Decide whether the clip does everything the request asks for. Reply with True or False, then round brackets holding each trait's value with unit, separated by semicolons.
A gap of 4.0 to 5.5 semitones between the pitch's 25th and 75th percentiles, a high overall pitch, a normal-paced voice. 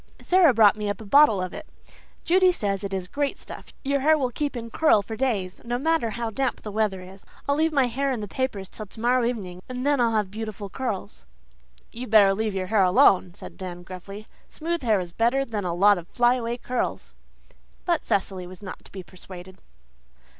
False (4.9 semitones; 220 Hz; 210 wpm)